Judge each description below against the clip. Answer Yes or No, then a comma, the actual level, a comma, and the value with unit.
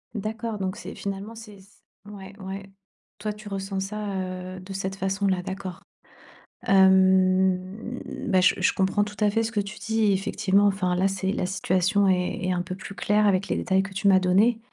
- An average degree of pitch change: No, narrow, 1.6 semitones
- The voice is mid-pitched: No, high, 195 Hz